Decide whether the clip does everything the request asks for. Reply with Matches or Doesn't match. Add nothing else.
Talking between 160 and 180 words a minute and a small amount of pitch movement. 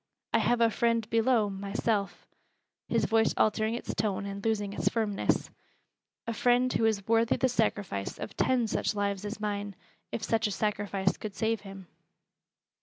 Matches